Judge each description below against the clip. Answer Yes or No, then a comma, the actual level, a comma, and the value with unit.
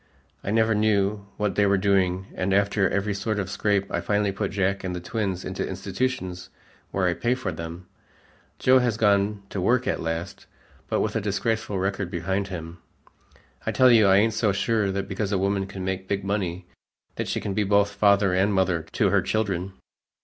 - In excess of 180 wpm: Yes, average, 200 wpm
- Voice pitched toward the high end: No, low, 100 Hz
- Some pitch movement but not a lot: No, narrow, 1.7 semitones